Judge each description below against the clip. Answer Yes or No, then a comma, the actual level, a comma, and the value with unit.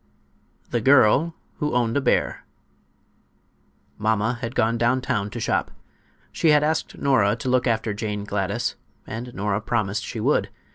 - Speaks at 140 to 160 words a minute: Yes, average, 150 wpm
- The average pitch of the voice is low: Yes, low, 115 Hz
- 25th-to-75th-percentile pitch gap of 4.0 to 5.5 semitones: No, average, 3.6 semitones